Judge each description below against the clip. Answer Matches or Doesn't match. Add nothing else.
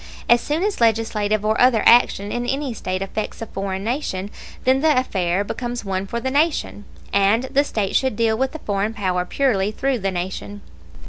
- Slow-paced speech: Doesn't match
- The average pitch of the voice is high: Matches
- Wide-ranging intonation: Doesn't match